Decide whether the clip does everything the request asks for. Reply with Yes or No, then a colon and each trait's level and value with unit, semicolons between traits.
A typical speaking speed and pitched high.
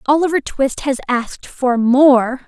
Yes: average, 145 wpm; very high, 265 Hz